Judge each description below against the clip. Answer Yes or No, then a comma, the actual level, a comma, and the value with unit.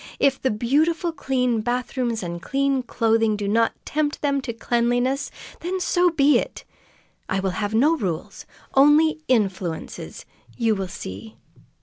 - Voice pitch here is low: No, high, 245 Hz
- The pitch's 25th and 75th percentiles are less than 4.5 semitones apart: No, average, 5.0 semitones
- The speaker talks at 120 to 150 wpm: Yes, average, 140 wpm